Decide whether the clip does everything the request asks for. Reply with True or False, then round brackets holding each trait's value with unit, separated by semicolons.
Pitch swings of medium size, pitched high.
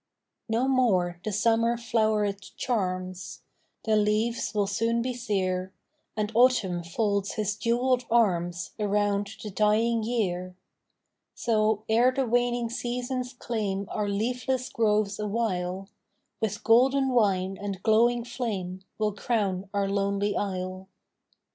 True (3.2 semitones; 215 Hz)